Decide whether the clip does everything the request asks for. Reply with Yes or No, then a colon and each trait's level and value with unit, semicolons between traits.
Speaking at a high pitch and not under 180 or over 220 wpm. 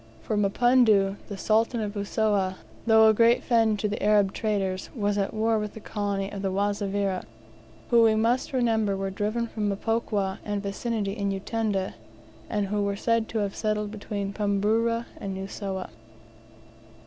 No: high, 205 Hz; average, 160 wpm